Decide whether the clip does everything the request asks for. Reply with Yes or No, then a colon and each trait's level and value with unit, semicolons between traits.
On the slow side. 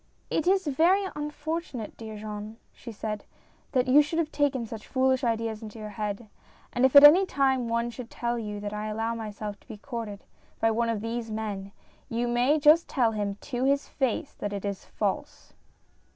No: average, 195 wpm